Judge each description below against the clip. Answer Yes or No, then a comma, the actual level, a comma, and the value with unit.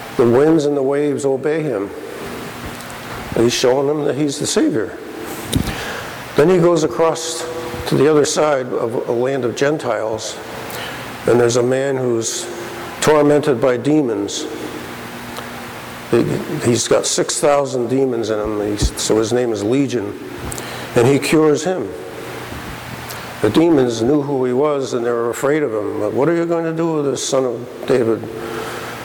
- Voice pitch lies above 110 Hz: Yes, low, 135 Hz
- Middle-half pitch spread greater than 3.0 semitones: Yes, average, 4.0 semitones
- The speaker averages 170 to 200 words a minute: No, average, 155 wpm